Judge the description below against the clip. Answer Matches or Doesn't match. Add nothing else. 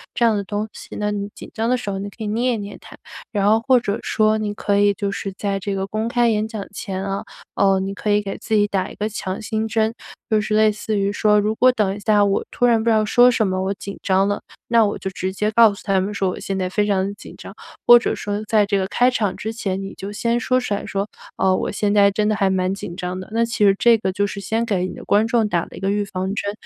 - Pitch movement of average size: Doesn't match